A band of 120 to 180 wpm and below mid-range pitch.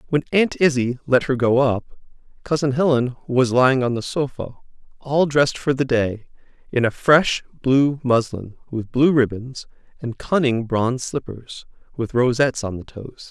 Yes: average, 160 wpm; low, 130 Hz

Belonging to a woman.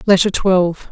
Yes: female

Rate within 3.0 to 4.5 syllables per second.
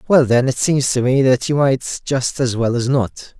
Yes: 4.4 syllables/s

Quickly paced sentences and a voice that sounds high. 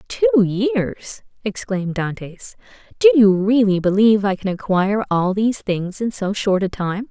No: average, 160 wpm; high, 200 Hz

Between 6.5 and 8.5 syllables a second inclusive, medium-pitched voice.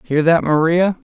No: 4.4 syllables/s; medium, 165 Hz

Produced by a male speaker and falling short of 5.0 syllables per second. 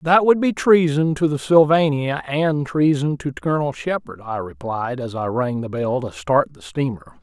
Yes: male; 4.7 syllables/s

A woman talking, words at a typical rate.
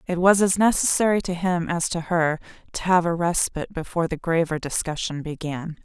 Yes: female; average, 185 wpm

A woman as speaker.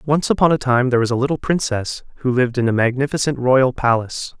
No: male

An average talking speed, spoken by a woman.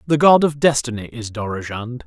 No: average, 175 wpm; male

